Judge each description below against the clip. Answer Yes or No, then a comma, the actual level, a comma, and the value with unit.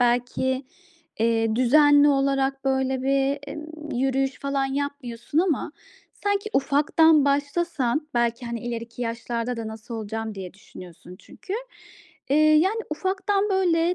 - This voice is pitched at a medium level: No, very high, 270 Hz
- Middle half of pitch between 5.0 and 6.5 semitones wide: No, average, 4.3 semitones